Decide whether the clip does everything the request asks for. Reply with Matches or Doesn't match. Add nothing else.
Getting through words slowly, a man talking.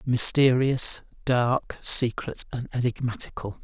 Matches